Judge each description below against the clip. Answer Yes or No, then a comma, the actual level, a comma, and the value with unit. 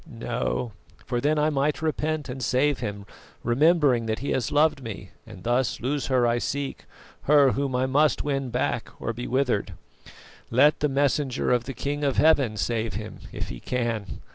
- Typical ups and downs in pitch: Yes, average, 3.5 semitones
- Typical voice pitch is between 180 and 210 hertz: No, low, 130 Hz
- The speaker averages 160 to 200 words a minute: Yes, average, 180 wpm